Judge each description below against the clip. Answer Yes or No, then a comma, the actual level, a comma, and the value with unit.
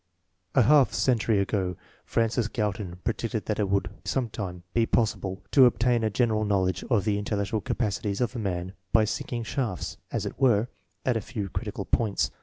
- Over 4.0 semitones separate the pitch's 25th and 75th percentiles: No, average, 3.2 semitones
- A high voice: No, low, 110 Hz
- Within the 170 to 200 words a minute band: Yes, average, 180 wpm